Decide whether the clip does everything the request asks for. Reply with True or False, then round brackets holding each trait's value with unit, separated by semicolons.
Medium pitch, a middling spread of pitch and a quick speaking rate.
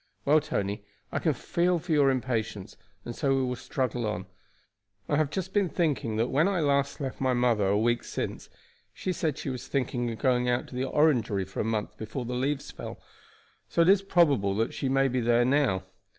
False (130 Hz; 4.2 semitones; 210 wpm)